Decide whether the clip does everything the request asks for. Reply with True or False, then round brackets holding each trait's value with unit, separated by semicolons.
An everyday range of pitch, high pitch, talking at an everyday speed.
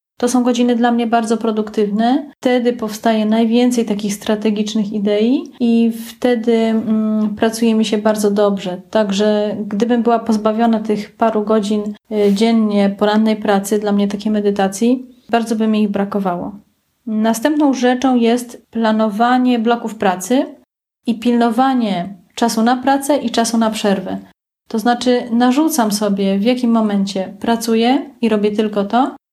False (2.3 semitones; 225 Hz; 135 wpm)